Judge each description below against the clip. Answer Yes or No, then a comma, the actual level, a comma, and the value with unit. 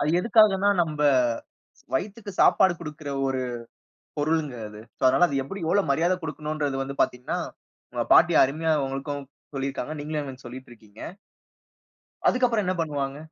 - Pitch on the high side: No, medium, 150 Hz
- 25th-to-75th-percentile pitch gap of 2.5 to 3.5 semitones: No, average, 4.3 semitones